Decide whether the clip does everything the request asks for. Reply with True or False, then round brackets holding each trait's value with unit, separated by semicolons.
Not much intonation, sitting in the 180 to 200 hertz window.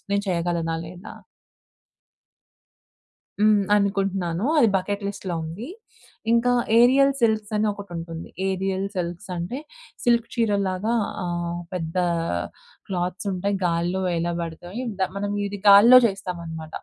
False (3.2 semitones; 190 Hz)